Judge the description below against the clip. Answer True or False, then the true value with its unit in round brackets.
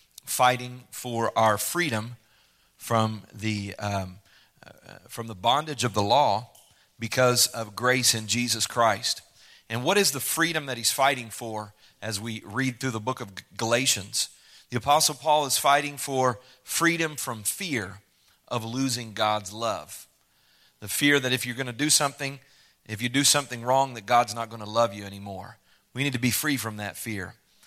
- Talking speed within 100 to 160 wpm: False (175 wpm)